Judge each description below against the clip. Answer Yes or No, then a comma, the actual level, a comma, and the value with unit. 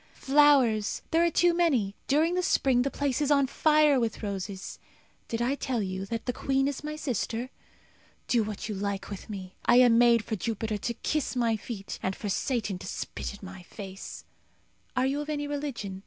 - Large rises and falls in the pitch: Yes, wide, 5.8 semitones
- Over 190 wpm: Yes, average, 200 wpm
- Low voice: No, high, 240 Hz